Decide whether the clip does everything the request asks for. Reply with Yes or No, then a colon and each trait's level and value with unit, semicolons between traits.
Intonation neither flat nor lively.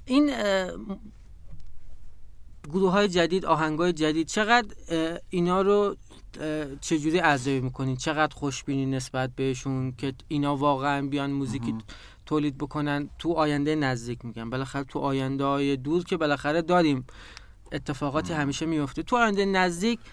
Yes: average, 4.1 semitones